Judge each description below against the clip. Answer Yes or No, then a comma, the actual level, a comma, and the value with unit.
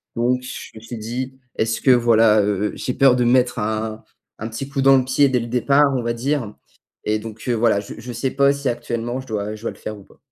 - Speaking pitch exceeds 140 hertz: No, low, 120 Hz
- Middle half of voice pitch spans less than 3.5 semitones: Yes, average, 2.8 semitones